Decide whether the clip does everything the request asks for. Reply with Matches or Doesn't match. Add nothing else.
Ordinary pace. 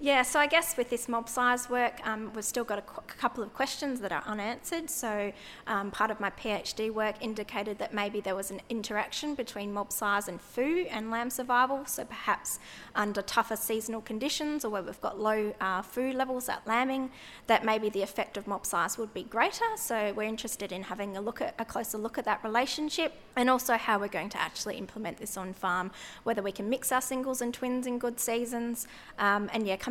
Doesn't match